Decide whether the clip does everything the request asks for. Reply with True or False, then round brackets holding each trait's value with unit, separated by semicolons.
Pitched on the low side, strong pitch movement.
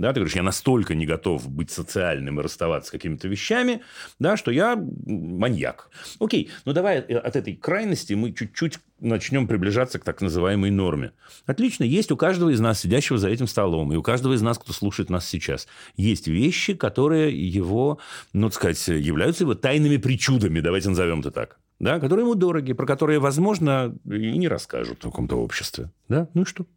True (115 Hz; 8.0 semitones)